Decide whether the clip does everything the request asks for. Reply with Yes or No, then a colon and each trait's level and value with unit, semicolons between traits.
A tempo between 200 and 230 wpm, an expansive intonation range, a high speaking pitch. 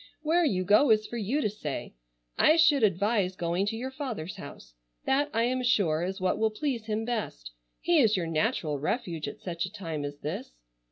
Yes: fast, 205 wpm; wide, 6.3 semitones; high, 210 Hz